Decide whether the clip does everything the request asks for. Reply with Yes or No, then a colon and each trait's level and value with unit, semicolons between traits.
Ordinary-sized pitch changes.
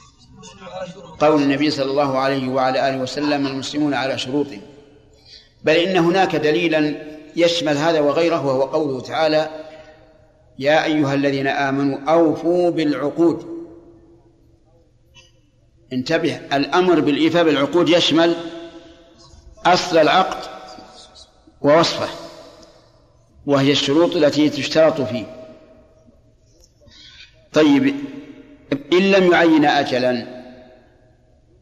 Yes: average, 3.5 semitones